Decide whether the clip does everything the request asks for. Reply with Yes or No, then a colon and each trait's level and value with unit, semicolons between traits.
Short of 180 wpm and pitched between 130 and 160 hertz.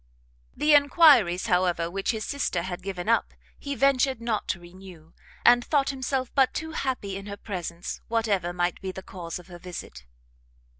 No: average, 170 wpm; high, 195 Hz